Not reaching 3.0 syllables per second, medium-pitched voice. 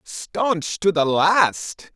Yes: 2.2 syllables/s; medium, 180 Hz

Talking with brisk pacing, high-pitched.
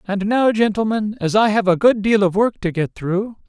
Yes: fast, 240 wpm; high, 210 Hz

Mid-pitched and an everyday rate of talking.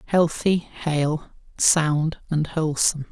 No: medium, 160 Hz; slow, 95 wpm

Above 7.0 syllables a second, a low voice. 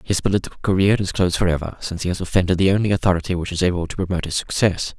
Yes: 7.9 syllables/s; very low, 90 Hz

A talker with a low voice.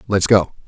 Yes: low, 100 Hz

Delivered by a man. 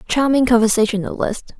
No: female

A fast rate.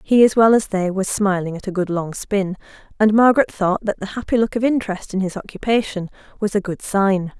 Yes: fast, 225 wpm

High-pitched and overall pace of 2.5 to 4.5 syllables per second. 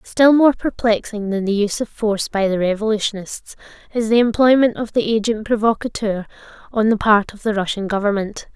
No: high, 215 Hz; 5.5 syllables/s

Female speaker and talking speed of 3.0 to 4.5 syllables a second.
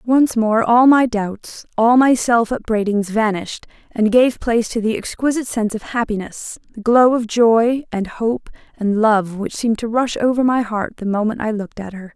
No: female; 5.0 syllables/s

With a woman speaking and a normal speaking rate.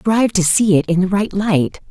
No: female; fast, 250 wpm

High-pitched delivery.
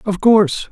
Yes: high, 200 Hz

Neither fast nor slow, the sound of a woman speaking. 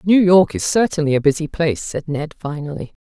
Yes: average, 195 wpm; female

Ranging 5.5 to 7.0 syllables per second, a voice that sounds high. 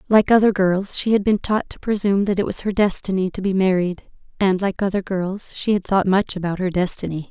Yes: 5.6 syllables/s; high, 195 Hz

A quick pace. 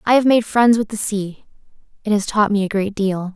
Yes: fast, 250 wpm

